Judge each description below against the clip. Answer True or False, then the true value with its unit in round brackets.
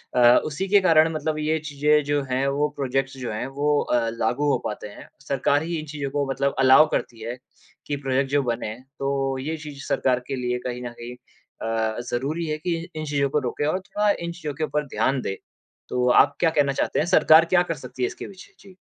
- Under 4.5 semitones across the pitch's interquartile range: True (3.3 semitones)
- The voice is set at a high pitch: False (140 Hz)